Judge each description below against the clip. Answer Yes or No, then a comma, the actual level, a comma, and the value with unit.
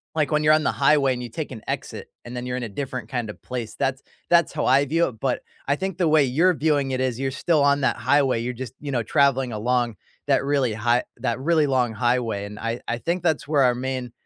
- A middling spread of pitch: Yes, average, 3.0 semitones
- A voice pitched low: Yes, low, 130 Hz